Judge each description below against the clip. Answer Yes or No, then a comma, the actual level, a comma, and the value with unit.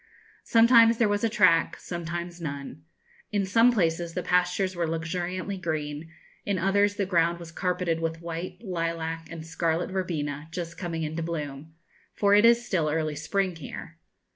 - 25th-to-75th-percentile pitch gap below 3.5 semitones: Yes, average, 2.7 semitones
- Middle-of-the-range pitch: Yes, medium, 170 Hz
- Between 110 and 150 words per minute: No, average, 160 wpm